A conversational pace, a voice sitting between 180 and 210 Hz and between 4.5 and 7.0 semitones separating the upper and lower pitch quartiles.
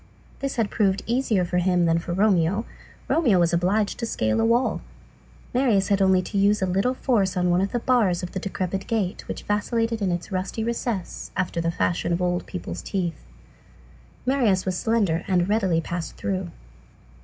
No: average, 190 wpm; high, 190 Hz; average, 3.8 semitones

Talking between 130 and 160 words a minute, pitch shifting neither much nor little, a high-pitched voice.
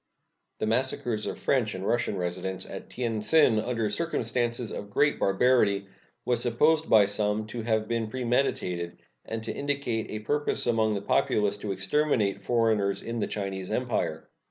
No: average, 155 wpm; average, 3.2 semitones; low, 110 Hz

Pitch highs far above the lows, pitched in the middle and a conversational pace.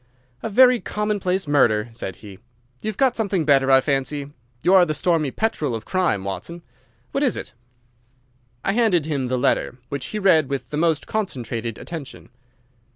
Yes: wide, 6.8 semitones; medium, 155 Hz; average, 170 wpm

